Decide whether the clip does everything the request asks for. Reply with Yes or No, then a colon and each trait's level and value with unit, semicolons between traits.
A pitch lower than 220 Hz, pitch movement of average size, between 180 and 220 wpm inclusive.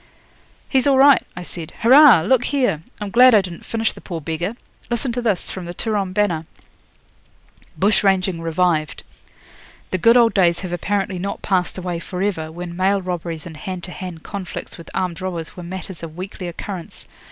Yes: medium, 185 Hz; average, 3.3 semitones; average, 185 wpm